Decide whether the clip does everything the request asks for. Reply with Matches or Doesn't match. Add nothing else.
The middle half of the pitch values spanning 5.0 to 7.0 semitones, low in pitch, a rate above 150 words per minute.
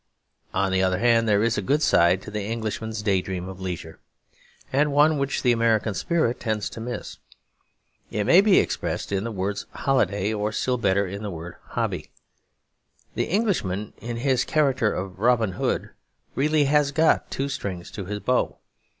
Matches